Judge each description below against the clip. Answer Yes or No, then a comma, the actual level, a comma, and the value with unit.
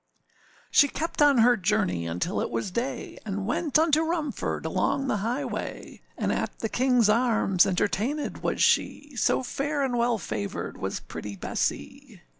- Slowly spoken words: No, average, 155 wpm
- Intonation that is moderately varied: No, wide, 6.5 semitones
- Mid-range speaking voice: No, high, 240 Hz